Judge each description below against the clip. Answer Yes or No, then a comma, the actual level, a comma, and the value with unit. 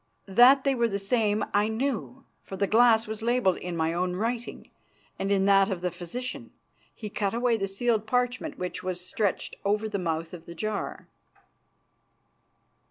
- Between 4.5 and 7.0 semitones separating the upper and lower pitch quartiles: No, average, 4.1 semitones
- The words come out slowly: No, average, 170 wpm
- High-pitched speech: Yes, high, 210 Hz